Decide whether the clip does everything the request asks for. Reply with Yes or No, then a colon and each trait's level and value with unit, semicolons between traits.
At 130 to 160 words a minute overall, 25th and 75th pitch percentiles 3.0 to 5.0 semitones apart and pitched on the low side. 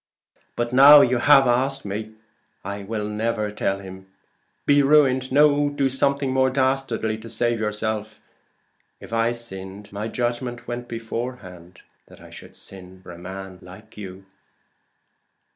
Yes: average, 145 wpm; average, 4.6 semitones; low, 115 Hz